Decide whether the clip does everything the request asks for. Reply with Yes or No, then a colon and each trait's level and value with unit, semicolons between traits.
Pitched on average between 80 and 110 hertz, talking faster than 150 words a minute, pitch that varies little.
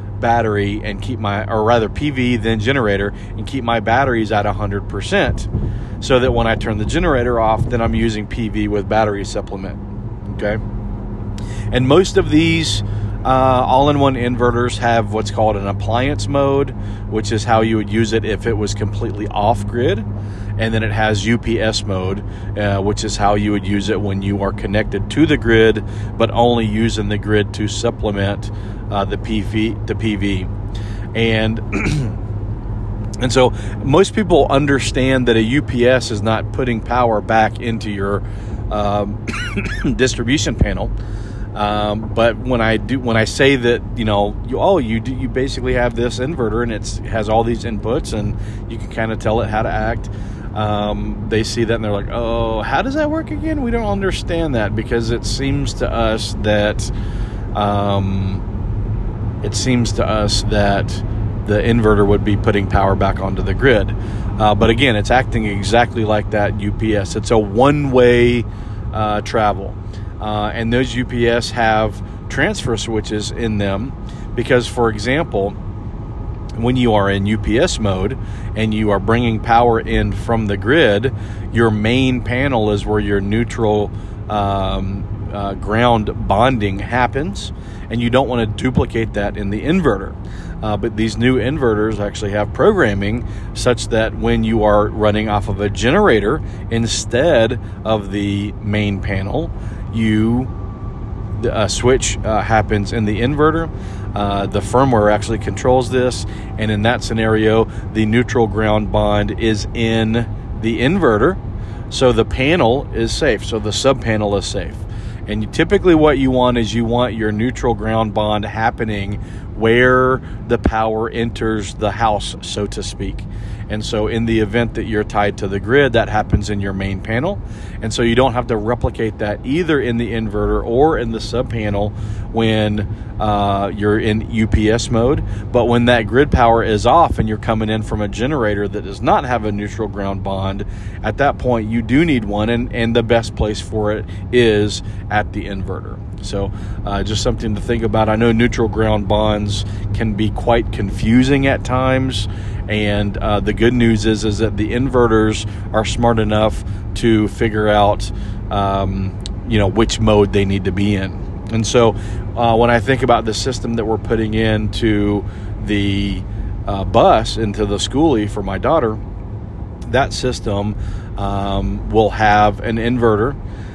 Yes: low, 105 Hz; average, 165 wpm; narrow, 2.0 semitones